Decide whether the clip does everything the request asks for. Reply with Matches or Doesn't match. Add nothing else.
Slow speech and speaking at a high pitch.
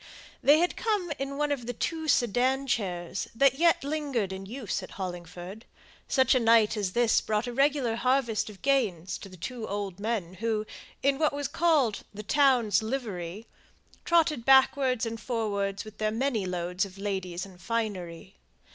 Doesn't match